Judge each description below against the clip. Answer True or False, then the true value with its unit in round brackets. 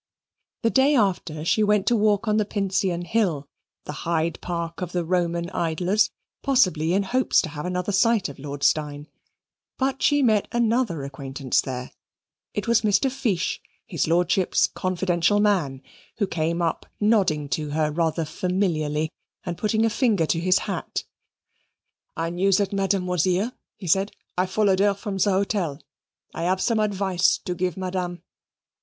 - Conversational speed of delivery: True (160 wpm)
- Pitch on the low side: False (185 Hz)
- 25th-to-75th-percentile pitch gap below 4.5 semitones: True (3.9 semitones)